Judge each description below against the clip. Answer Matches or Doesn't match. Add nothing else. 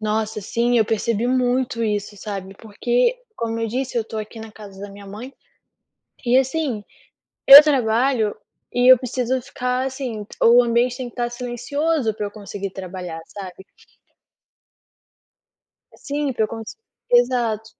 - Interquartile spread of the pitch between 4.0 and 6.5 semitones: Doesn't match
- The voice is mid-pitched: Doesn't match